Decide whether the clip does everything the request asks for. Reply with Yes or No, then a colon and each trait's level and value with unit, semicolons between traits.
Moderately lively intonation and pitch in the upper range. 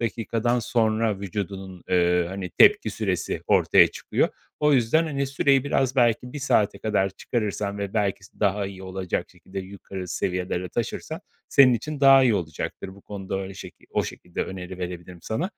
No: average, 4.2 semitones; low, 100 Hz